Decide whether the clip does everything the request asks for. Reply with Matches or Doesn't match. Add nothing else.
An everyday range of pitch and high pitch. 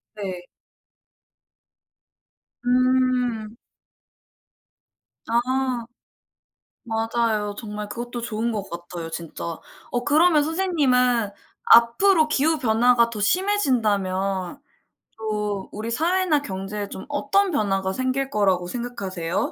Matches